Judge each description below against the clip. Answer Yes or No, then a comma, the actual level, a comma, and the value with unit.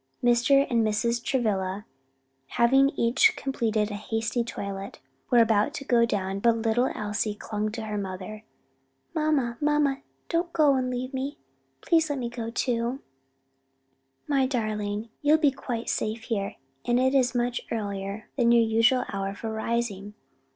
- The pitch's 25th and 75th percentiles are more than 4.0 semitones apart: No, average, 3.5 semitones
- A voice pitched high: Yes, high, 235 Hz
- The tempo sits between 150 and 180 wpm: Yes, average, 155 wpm